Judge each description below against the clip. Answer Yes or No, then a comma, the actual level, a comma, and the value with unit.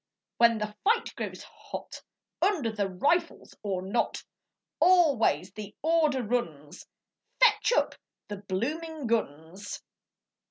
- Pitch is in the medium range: No, high, 230 Hz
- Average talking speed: No, slow, 110 wpm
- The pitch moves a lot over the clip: Yes, wide, 8.5 semitones